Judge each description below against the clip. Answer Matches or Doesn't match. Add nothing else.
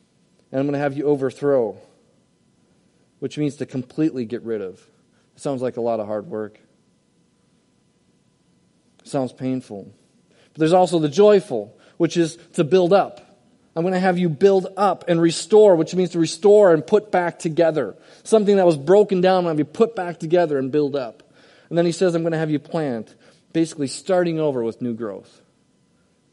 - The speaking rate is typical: Matches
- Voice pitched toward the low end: Doesn't match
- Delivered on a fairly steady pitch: Doesn't match